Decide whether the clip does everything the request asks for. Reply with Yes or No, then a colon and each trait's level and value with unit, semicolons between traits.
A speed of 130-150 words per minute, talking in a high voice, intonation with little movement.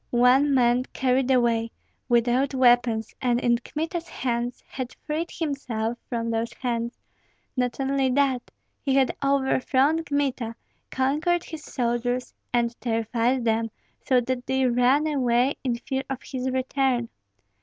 Yes: slow, 135 wpm; very high, 255 Hz; narrow, 2.2 semitones